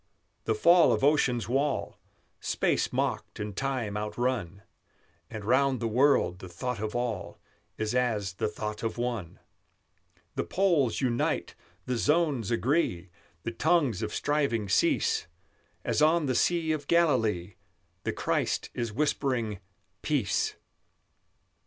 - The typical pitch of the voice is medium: No, low, 120 Hz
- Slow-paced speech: Yes, slow, 125 wpm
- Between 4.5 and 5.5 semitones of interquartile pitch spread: Yes, average, 5.1 semitones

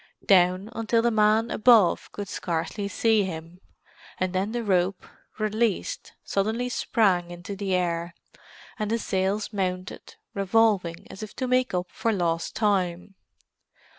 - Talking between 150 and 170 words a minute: No, slow, 135 wpm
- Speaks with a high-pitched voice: Yes, high, 200 Hz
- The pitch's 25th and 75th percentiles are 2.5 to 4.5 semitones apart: Yes, average, 3.3 semitones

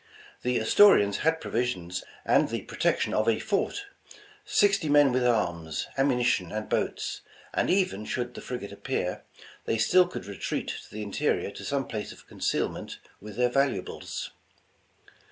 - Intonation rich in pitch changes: Yes, wide, 5.9 semitones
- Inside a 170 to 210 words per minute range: No, average, 155 wpm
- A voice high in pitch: No, low, 120 Hz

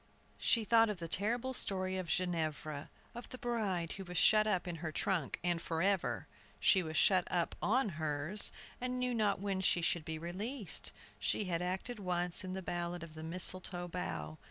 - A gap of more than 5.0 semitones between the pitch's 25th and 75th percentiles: No, average, 3.7 semitones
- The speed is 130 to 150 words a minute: No, average, 185 wpm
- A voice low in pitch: No, medium, 180 Hz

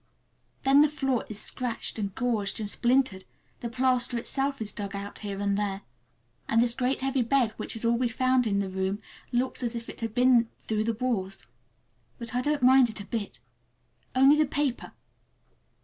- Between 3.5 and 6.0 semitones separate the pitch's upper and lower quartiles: Yes, average, 3.9 semitones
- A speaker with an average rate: Yes, average, 185 wpm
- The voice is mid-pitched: No, high, 235 Hz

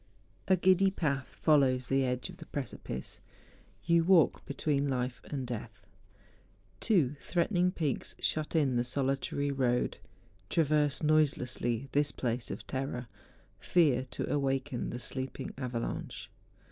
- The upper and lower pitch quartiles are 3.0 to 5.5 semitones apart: Yes, average, 3.5 semitones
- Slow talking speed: Yes, slow, 125 wpm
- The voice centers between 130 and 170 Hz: Yes, low, 135 Hz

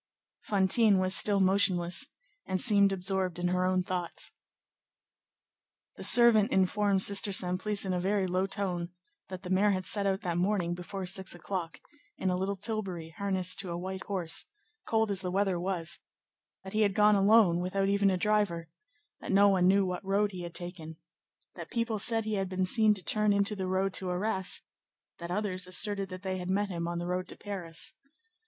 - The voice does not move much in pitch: Yes, narrow, 1.9 semitones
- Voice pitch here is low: No, high, 190 Hz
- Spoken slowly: No, average, 190 wpm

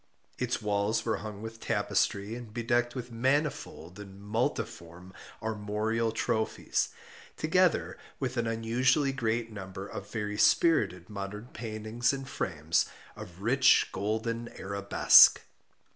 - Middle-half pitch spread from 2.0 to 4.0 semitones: Yes, average, 2.7 semitones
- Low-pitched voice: Yes, low, 110 Hz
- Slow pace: Yes, slow, 115 wpm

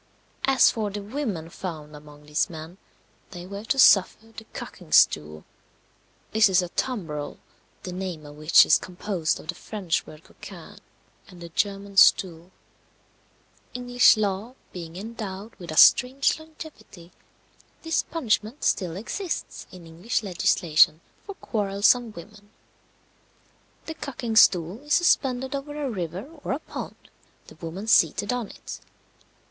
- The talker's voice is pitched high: Yes, high, 200 Hz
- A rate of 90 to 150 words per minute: Yes, average, 140 wpm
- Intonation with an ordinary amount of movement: No, wide, 6.0 semitones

